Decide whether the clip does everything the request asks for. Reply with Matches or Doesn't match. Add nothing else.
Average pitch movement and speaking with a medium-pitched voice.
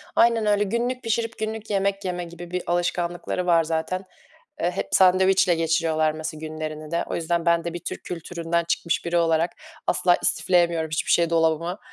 Doesn't match